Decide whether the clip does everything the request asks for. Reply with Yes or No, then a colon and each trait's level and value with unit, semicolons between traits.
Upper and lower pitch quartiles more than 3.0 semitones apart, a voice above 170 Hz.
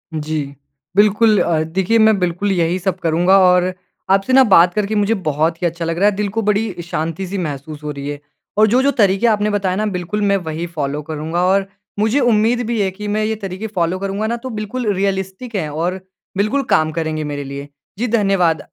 Yes: average, 4.3 semitones; high, 190 Hz